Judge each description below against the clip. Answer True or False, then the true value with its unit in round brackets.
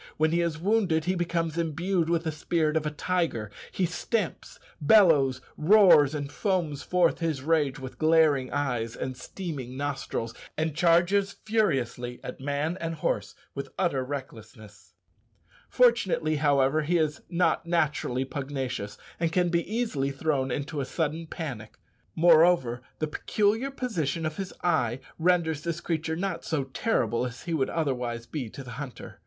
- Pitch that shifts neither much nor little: True (4.3 semitones)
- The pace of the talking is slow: False (155 wpm)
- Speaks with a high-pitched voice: False (155 Hz)